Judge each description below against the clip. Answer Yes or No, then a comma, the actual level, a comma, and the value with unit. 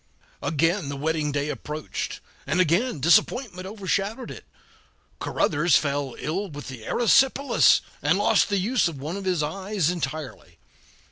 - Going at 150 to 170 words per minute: No, average, 140 wpm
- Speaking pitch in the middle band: Yes, medium, 165 Hz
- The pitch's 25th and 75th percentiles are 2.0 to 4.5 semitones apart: No, average, 5.2 semitones